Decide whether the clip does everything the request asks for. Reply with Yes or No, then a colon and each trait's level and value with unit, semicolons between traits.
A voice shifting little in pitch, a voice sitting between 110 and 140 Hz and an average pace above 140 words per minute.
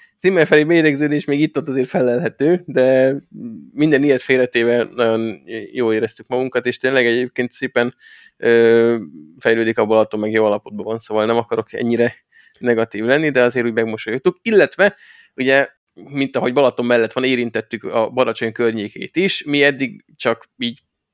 No: average, 3.7 semitones; low, 125 Hz; average, 150 wpm